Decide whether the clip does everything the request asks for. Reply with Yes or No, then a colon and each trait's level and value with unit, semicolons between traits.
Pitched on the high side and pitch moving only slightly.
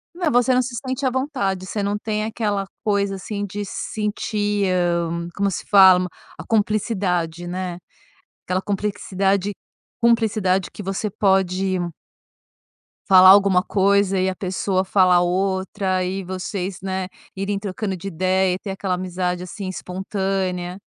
Yes: high, 195 Hz; narrow, 1.9 semitones